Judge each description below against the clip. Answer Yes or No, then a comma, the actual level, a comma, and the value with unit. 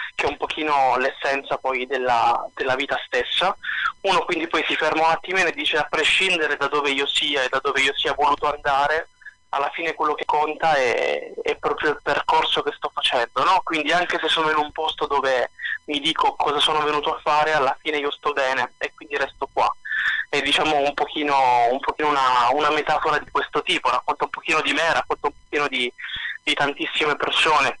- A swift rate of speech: Yes, fast, 200 wpm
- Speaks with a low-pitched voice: No, medium, 150 Hz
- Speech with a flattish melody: Yes, narrow, 2.1 semitones